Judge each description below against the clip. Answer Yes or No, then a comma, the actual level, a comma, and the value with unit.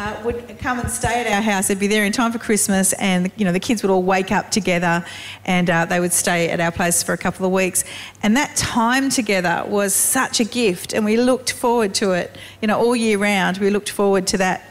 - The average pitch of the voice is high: Yes, high, 200 Hz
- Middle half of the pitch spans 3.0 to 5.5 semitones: Yes, average, 3.6 semitones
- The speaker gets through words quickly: Yes, fast, 255 wpm